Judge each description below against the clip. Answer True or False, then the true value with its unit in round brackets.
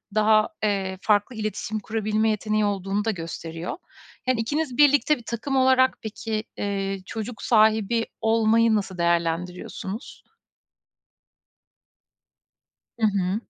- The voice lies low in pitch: False (215 Hz)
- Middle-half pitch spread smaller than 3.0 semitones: True (2.6 semitones)